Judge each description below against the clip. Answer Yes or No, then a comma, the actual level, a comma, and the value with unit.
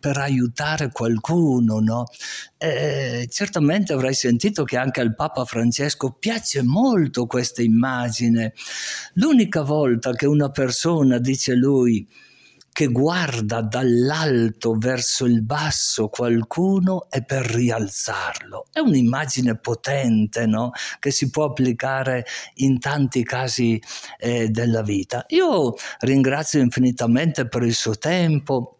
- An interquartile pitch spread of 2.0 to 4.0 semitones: Yes, average, 3.4 semitones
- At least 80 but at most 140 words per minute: Yes, slow, 115 wpm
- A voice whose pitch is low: Yes, low, 130 Hz